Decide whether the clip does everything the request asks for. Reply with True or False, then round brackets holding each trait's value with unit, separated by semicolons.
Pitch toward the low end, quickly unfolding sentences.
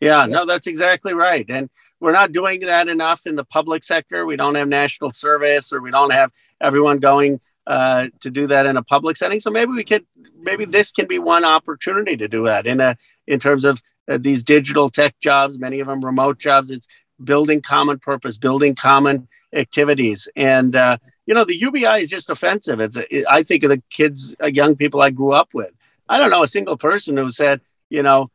False (145 Hz; 215 wpm)